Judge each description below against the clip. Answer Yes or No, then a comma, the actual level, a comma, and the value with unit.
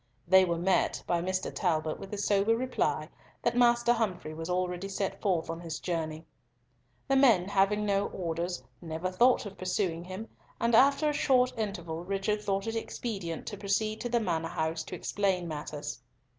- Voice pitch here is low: No, high, 190 Hz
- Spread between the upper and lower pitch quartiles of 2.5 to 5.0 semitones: Yes, average, 4.1 semitones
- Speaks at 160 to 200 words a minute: Yes, average, 175 wpm